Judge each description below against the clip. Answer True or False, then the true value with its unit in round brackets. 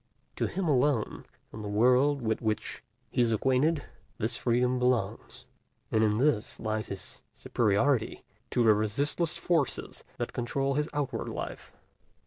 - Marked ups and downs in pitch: False (4.4 semitones)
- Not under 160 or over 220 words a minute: False (140 wpm)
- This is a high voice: False (125 Hz)